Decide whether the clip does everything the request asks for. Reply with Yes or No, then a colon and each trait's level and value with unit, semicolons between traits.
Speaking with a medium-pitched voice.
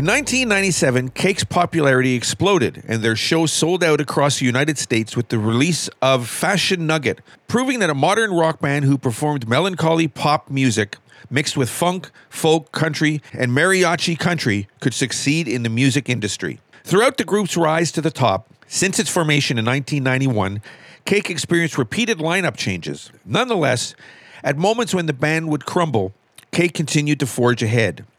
Yes: medium, 150 Hz